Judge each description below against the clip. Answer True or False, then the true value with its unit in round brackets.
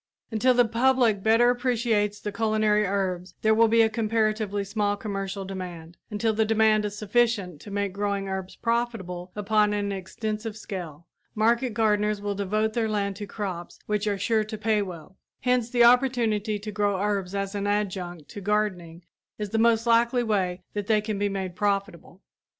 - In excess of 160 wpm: True (175 wpm)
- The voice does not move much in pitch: True (2.2 semitones)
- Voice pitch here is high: True (210 Hz)